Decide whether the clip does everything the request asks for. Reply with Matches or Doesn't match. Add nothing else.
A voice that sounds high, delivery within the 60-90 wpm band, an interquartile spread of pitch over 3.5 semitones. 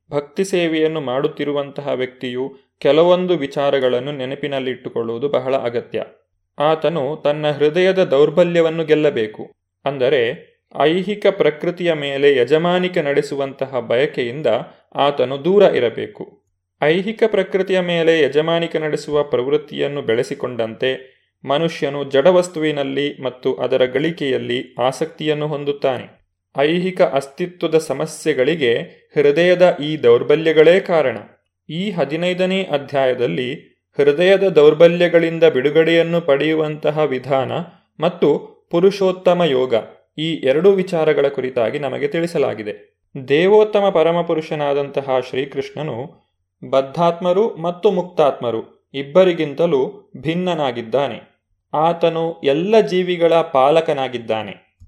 Doesn't match